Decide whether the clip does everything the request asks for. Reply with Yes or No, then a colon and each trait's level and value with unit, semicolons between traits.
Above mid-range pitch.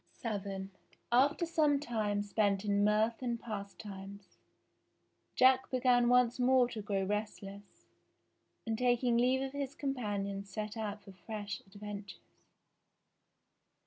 Yes: high, 215 Hz